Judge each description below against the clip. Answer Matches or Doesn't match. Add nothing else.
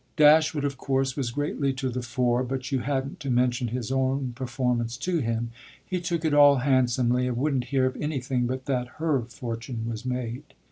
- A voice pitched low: Matches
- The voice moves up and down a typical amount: Doesn't match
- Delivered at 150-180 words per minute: Doesn't match